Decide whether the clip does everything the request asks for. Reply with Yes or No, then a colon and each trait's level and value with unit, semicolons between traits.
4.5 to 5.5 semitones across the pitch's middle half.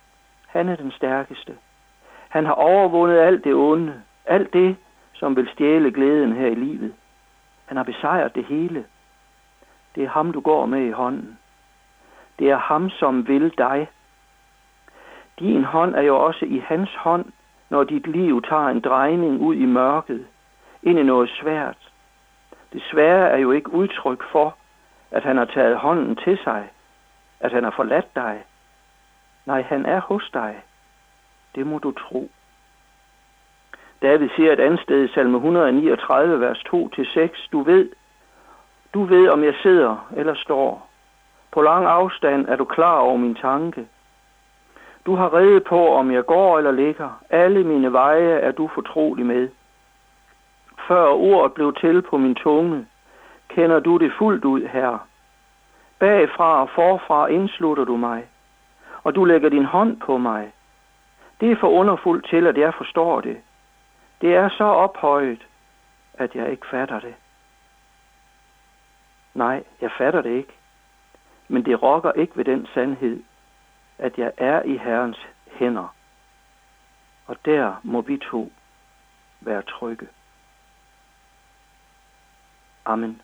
Yes: average, 5.2 semitones